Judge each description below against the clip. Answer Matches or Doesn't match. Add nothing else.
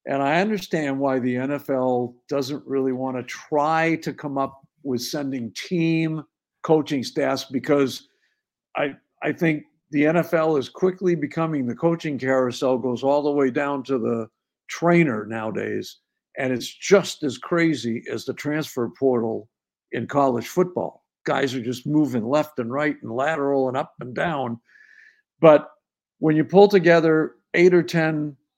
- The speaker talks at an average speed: Matches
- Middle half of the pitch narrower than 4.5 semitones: Matches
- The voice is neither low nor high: Matches